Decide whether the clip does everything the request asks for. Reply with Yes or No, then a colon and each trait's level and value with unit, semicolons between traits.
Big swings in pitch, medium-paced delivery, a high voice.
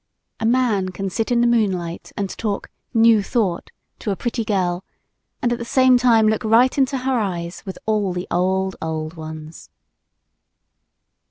No: average, 4.6 semitones; average, 165 wpm; high, 210 Hz